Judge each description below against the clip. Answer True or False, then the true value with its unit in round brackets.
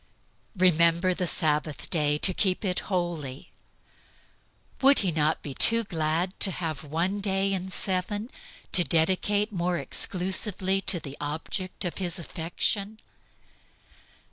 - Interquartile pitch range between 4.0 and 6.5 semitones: False (3.1 semitones)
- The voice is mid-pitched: True (180 Hz)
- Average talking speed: False (125 wpm)